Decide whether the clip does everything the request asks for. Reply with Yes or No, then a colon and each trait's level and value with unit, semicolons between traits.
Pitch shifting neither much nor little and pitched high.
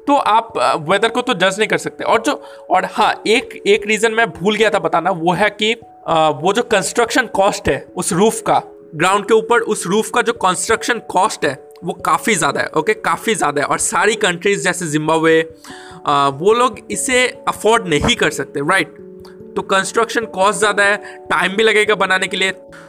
Yes: average, 3.6 semitones; high, 205 Hz